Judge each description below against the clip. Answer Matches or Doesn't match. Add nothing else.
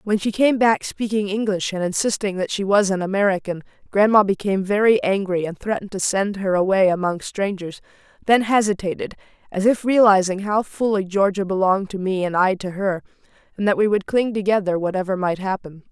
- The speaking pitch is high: Matches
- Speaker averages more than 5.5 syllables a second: Matches